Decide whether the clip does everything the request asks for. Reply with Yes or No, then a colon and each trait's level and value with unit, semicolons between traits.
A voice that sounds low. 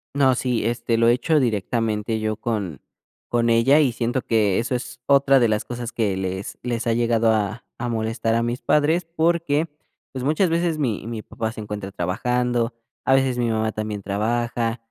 Yes: low, 115 Hz